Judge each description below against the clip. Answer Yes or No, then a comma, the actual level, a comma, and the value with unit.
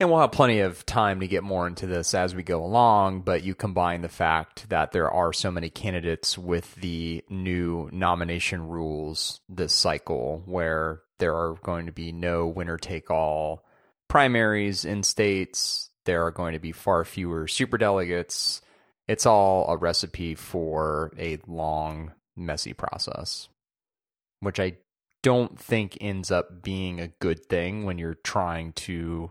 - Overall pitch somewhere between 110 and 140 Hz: No, very low, 90 Hz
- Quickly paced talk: No, average, 160 wpm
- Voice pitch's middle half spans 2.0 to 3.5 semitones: Yes, average, 2.7 semitones